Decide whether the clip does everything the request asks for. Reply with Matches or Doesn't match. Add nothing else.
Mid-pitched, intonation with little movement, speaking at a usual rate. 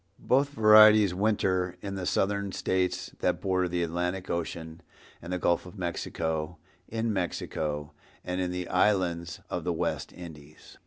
Doesn't match